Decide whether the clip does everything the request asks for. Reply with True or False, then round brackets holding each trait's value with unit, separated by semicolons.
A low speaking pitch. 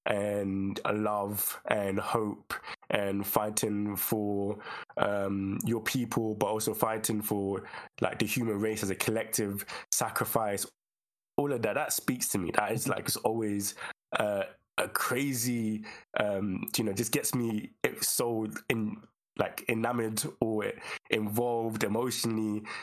True (110 Hz)